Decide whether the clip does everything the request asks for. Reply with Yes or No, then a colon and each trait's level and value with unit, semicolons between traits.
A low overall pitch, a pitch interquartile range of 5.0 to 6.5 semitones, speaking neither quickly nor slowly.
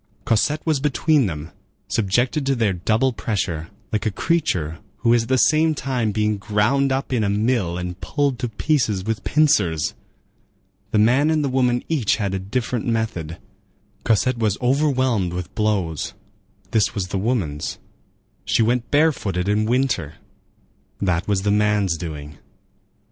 Yes: low, 110 Hz; wide, 5.5 semitones; average, 150 wpm